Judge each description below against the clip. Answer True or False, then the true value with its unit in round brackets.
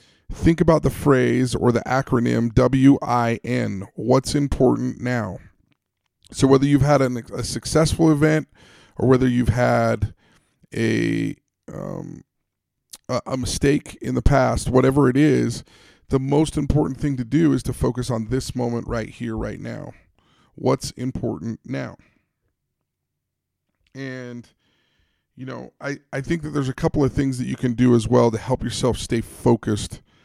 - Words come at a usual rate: True (155 wpm)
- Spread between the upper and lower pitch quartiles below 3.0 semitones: True (2.6 semitones)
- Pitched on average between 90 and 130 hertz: True (125 Hz)